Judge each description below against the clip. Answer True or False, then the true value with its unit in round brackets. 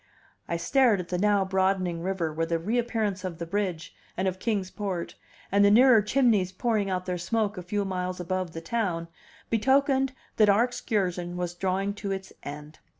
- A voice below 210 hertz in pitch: True (190 Hz)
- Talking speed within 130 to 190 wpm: True (185 wpm)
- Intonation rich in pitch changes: False (3.0 semitones)